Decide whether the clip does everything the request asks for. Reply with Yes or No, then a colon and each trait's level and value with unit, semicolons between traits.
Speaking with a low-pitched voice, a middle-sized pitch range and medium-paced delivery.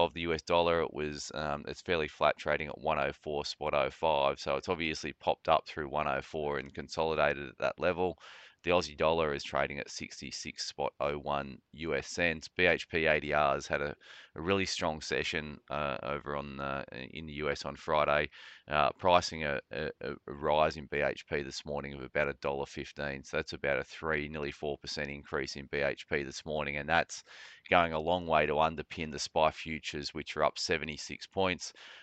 No: very low, 75 Hz; narrow, 2.0 semitones; average, 180 wpm